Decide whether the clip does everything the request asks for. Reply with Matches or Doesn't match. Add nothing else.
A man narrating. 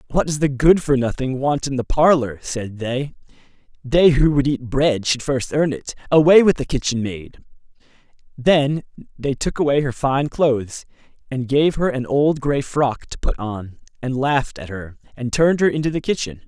Matches